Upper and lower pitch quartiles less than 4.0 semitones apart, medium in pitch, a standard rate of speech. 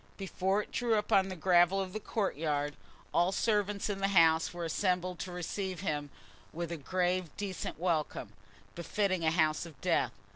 Yes: average, 3.0 semitones; medium, 180 Hz; average, 180 wpm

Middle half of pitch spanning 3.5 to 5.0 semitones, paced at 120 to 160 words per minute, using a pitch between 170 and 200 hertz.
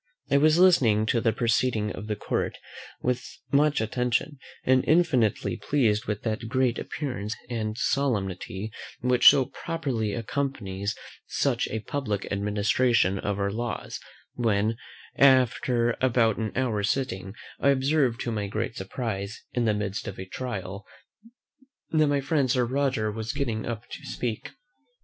No: average, 3.8 semitones; average, 145 wpm; low, 115 Hz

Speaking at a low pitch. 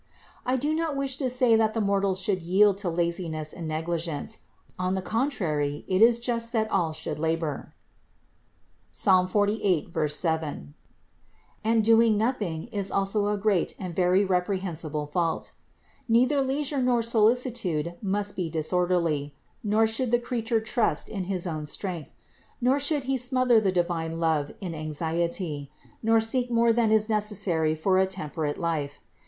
No: high, 195 Hz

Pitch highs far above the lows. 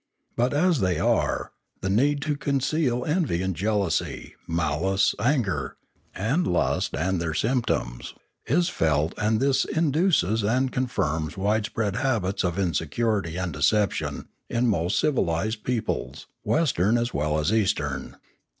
Yes: wide, 7.1 semitones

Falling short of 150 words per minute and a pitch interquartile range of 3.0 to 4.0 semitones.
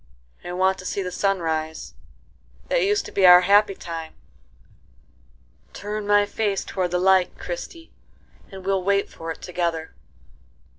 Yes: average, 140 wpm; average, 3.6 semitones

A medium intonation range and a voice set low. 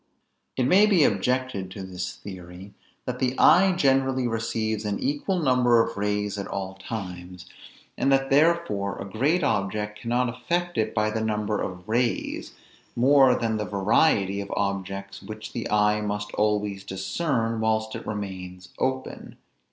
Yes: average, 4.4 semitones; low, 110 Hz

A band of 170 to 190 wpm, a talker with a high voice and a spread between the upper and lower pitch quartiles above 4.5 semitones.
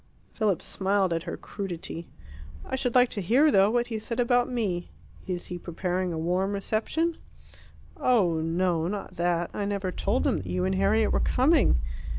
Yes: average, 175 wpm; high, 195 Hz; average, 5.1 semitones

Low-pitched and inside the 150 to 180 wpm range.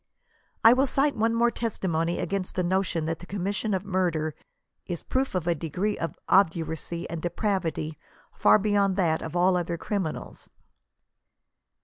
No: medium, 185 Hz; average, 155 wpm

